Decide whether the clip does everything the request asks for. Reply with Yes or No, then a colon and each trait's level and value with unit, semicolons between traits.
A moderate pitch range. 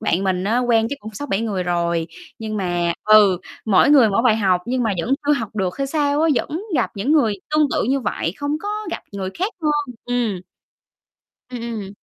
No: wide, 6.1 semitones